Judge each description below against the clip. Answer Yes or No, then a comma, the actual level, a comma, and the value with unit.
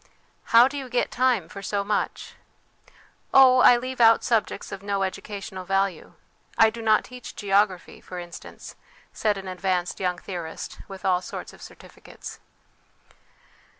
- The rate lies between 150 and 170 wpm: Yes, average, 160 wpm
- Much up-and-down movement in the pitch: No, average, 3.8 semitones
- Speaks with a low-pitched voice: No, high, 200 Hz